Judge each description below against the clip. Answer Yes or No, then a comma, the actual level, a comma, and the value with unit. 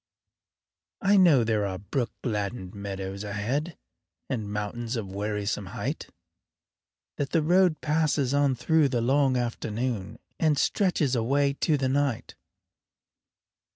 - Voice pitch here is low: Yes, low, 125 Hz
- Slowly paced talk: Yes, slow, 120 wpm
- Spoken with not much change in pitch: No, wide, 5.6 semitones